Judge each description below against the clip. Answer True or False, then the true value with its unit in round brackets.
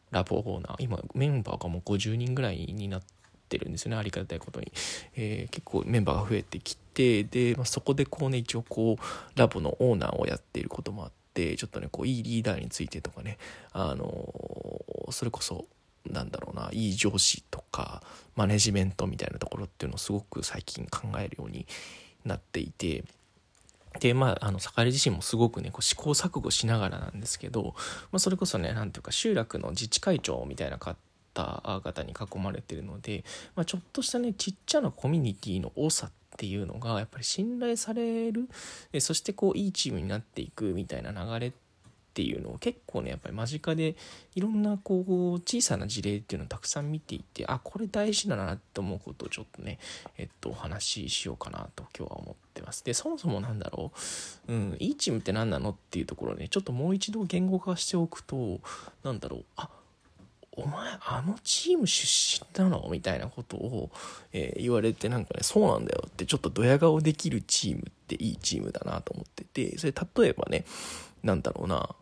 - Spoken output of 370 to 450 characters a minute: True (400 characters per minute)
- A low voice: True (120 Hz)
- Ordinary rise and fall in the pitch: False (8.8 semitones)